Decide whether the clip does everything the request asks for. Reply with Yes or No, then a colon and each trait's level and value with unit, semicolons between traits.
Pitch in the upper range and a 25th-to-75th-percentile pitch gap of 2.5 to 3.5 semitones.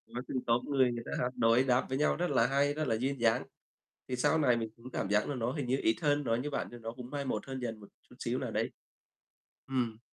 No: low, 125 Hz; average, 3.1 semitones